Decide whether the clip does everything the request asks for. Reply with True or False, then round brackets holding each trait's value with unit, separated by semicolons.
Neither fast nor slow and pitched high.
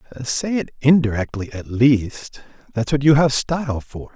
False (160 wpm; 130 Hz)